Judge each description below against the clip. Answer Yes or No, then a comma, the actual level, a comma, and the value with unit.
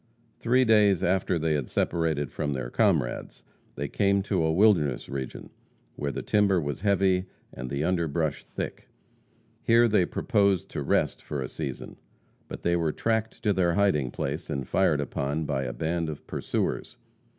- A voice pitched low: Yes, very low, 80 Hz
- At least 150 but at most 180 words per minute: Yes, average, 165 wpm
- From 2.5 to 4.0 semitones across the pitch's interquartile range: No, wide, 5.5 semitones